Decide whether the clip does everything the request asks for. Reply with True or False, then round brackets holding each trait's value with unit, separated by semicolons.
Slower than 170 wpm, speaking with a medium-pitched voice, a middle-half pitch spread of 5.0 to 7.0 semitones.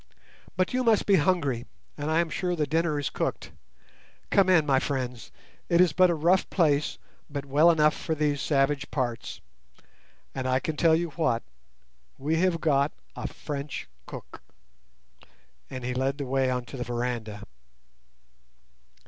False (155 wpm; 145 Hz; 4.0 semitones)